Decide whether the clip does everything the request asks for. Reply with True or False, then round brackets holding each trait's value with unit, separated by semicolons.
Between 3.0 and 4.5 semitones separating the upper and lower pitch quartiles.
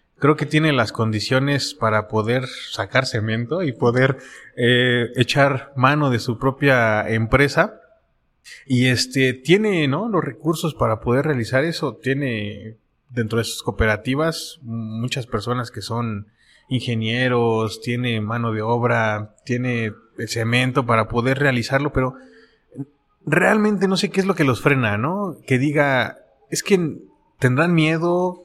True (4.0 semitones)